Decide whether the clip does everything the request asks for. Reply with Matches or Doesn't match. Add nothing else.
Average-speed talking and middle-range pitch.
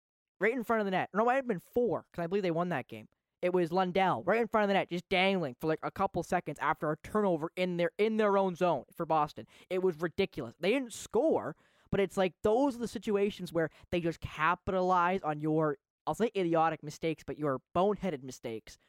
Doesn't match